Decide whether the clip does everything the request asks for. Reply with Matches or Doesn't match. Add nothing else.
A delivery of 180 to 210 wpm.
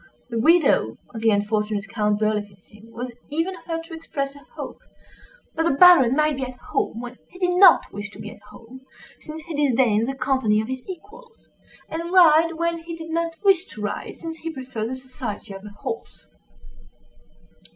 Matches